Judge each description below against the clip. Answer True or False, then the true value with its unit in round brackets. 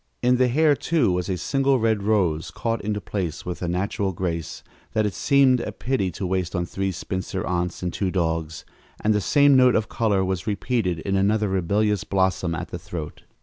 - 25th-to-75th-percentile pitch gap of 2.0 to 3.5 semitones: False (3.9 semitones)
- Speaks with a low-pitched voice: True (95 Hz)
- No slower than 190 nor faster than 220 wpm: True (200 wpm)